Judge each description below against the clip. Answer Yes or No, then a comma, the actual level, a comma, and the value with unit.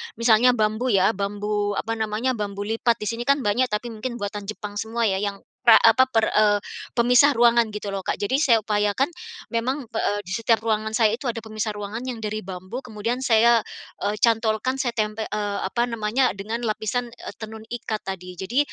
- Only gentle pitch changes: Yes, narrow, 2.3 semitones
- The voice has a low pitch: No, high, 220 Hz